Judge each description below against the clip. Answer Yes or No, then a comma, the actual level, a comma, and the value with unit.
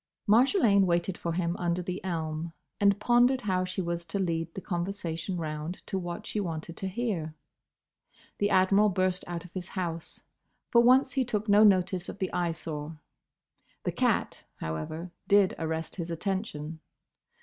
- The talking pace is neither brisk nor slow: Yes, average, 160 wpm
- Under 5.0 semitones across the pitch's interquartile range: Yes, average, 3.2 semitones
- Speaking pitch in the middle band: Yes, medium, 180 Hz